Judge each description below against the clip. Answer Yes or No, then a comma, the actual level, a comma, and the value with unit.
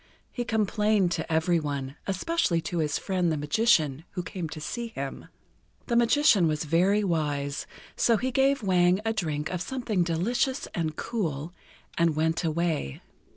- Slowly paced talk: No, average, 155 wpm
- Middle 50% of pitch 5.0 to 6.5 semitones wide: Yes, wide, 5.6 semitones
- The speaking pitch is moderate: Yes, medium, 175 Hz